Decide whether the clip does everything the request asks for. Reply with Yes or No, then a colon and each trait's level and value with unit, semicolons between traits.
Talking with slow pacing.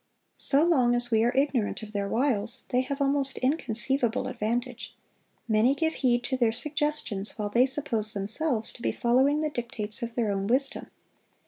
No: average, 175 wpm